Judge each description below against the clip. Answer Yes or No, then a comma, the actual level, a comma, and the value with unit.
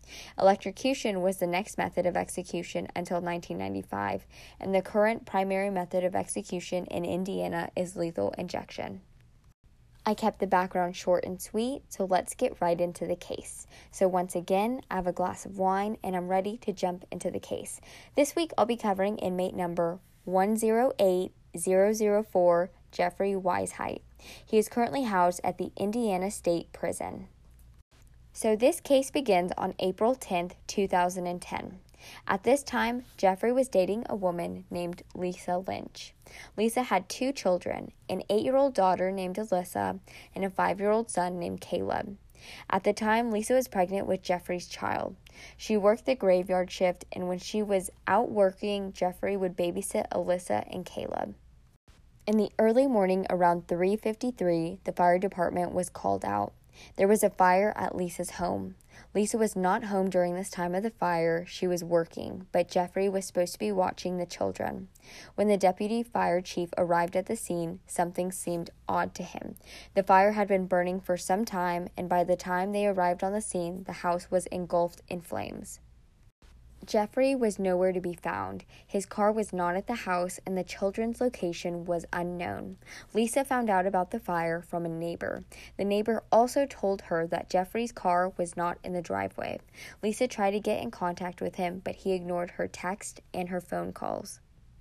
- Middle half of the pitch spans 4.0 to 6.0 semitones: No, average, 2.8 semitones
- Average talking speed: Yes, average, 170 wpm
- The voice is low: No, medium, 185 Hz